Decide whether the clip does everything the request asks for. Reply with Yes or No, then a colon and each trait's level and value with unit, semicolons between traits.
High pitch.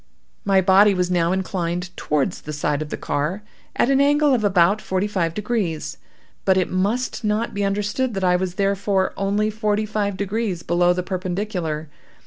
Yes: high, 195 Hz